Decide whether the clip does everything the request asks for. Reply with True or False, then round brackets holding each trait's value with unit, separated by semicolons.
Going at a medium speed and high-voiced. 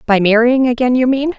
False (215 wpm; 245 Hz)